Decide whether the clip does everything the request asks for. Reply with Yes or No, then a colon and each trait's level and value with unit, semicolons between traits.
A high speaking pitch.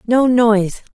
Yes: high, 230 Hz